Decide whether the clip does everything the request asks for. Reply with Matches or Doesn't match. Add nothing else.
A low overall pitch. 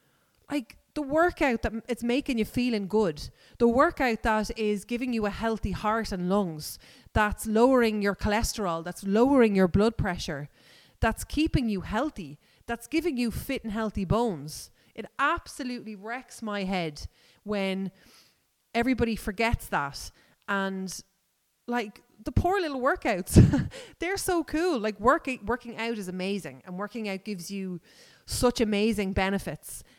Doesn't match